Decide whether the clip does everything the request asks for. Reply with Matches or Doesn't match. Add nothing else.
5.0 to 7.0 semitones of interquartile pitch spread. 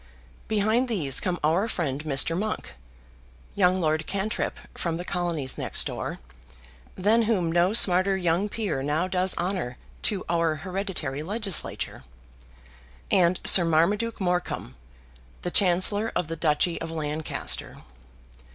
Doesn't match